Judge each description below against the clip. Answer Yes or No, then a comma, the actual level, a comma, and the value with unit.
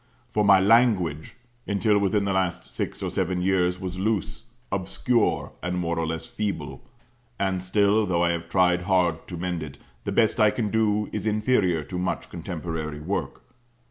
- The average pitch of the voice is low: Yes, very low, 95 Hz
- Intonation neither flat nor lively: Yes, average, 3.1 semitones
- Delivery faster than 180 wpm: No, average, 175 wpm